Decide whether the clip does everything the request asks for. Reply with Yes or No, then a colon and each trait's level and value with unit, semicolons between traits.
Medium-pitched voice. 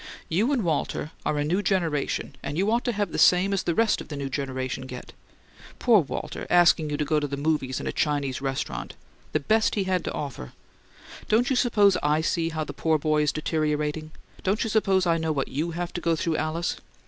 Yes: medium, 160 Hz